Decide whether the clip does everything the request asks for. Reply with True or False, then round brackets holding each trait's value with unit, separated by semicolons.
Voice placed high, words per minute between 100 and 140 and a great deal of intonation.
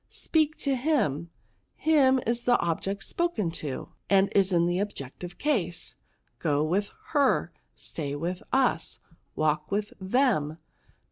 True (195 Hz; 135 wpm; 7.8 semitones)